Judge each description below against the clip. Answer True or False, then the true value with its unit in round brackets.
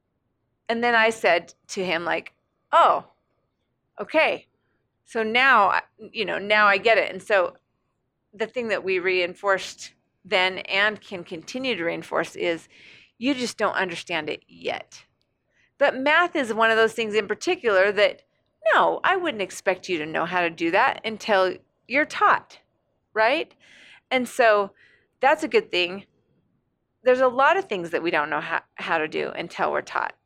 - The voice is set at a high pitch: True (210 Hz)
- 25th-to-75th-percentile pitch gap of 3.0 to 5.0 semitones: False (5.5 semitones)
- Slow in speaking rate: False (165 wpm)